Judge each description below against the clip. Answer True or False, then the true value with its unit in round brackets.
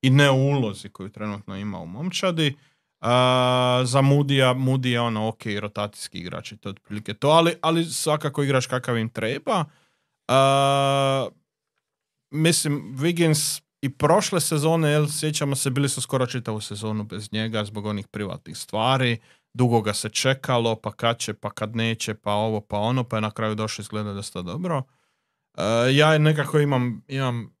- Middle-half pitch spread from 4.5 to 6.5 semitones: True (5.0 semitones)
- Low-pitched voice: True (125 Hz)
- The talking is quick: True (165 wpm)